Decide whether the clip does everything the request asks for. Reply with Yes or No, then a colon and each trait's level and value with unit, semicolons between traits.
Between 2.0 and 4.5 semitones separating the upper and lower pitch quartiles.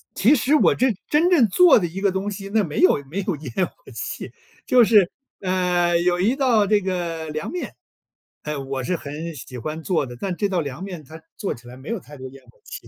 No: average, 5.2 semitones